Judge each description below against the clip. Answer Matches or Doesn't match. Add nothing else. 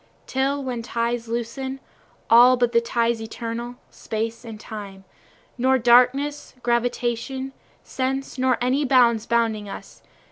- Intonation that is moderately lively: Doesn't match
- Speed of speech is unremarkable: Doesn't match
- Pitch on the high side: Matches